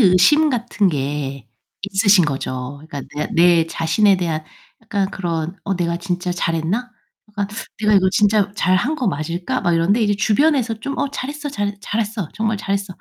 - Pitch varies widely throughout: No, average, 4.4 semitones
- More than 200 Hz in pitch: No, high, 195 Hz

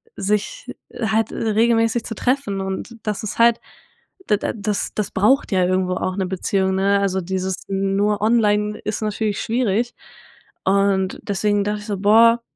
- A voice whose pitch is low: No, high, 205 Hz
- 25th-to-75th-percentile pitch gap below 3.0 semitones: Yes, narrow, 2.5 semitones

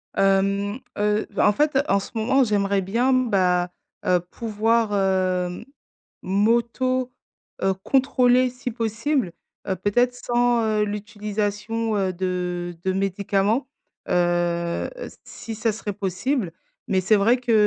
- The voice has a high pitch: Yes, high, 205 Hz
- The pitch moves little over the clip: No, average, 3.7 semitones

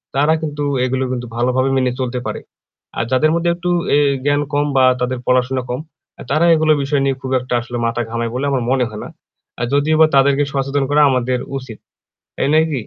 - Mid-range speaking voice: No, low, 130 Hz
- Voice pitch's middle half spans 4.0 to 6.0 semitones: No, narrow, 2.6 semitones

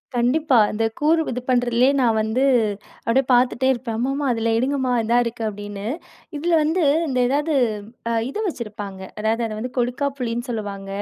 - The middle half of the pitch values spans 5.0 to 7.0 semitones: No, average, 3.1 semitones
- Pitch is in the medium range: No, high, 245 Hz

